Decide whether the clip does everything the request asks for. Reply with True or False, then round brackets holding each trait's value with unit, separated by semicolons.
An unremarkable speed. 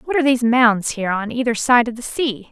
False (265 wpm)